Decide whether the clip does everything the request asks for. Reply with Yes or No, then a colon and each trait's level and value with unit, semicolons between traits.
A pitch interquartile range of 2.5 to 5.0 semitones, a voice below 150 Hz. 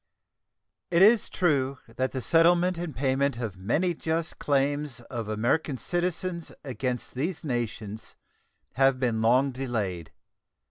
No: wide, 5.5 semitones; low, 135 Hz